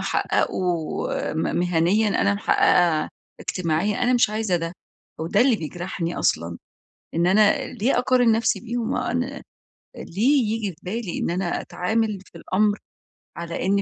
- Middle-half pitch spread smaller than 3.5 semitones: No, average, 4.7 semitones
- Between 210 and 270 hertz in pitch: No, high, 200 Hz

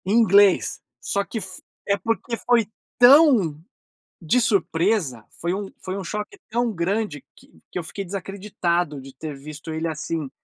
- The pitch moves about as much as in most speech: Yes, average, 4.8 semitones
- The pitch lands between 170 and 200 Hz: Yes, high, 190 Hz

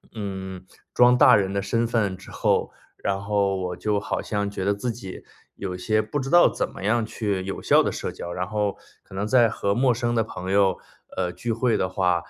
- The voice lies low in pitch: Yes, low, 100 Hz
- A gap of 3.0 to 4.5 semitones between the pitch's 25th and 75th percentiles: Yes, average, 3.3 semitones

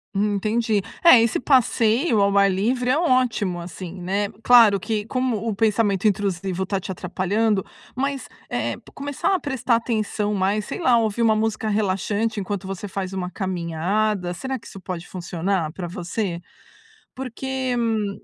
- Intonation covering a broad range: No, average, 3.4 semitones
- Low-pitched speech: No, high, 210 Hz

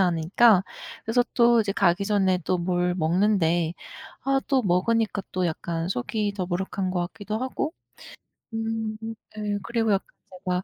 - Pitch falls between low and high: No, high, 195 Hz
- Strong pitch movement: No, average, 3.9 semitones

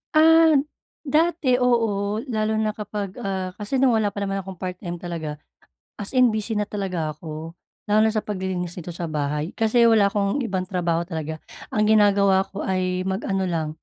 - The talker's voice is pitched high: Yes, high, 195 Hz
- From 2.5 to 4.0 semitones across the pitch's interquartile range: Yes, average, 3.5 semitones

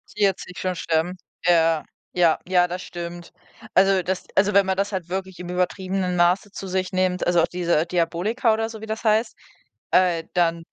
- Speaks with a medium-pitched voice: Yes, medium, 180 Hz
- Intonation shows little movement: Yes, narrow, 1.9 semitones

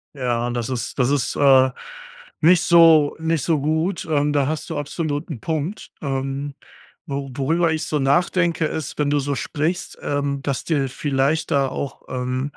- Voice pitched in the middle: Yes, medium, 145 Hz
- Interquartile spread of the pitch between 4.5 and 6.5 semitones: No, average, 2.8 semitones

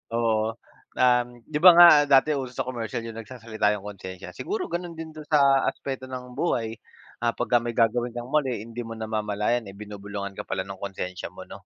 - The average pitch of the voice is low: Yes, low, 120 Hz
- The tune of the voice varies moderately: Yes, average, 3.7 semitones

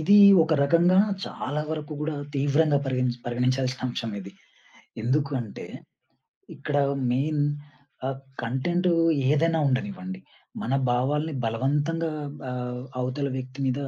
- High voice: No, medium, 140 Hz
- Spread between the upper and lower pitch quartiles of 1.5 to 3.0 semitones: No, average, 3.8 semitones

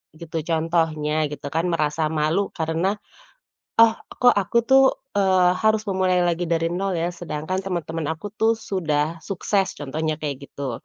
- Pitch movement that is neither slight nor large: Yes, average, 3.7 semitones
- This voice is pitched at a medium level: Yes, medium, 170 Hz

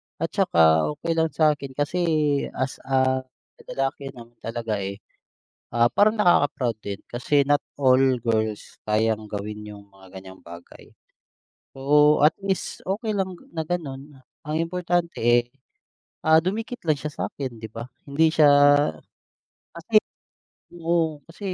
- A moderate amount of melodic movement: No, wide, 6.4 semitones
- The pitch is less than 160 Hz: Yes, medium, 140 Hz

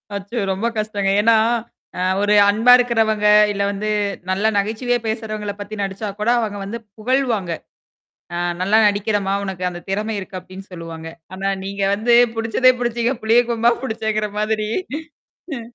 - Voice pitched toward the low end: No, high, 215 Hz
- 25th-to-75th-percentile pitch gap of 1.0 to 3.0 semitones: Yes, narrow, 2.4 semitones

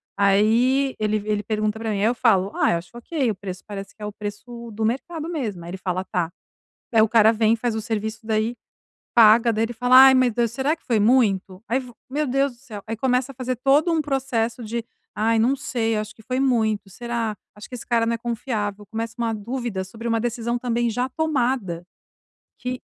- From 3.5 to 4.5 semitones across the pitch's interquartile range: No, average, 2.9 semitones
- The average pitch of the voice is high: Yes, high, 230 Hz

